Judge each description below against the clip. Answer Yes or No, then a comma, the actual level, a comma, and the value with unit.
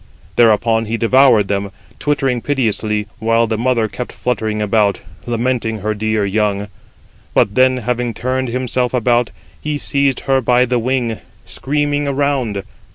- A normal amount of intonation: Yes, average, 3.0 semitones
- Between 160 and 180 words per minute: No, average, 140 wpm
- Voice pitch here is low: Yes, low, 120 Hz